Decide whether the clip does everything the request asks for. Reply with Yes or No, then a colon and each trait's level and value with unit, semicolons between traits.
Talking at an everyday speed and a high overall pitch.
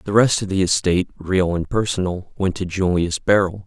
No: average, 195 wpm; very low, 95 Hz